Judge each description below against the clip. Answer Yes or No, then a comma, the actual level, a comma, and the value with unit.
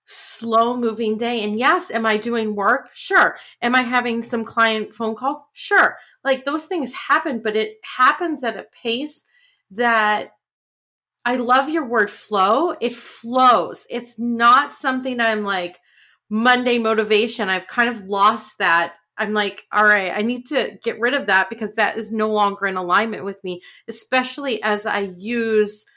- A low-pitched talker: No, high, 230 Hz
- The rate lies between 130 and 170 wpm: Yes, average, 165 wpm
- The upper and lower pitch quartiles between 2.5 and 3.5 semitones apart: Yes, average, 3.0 semitones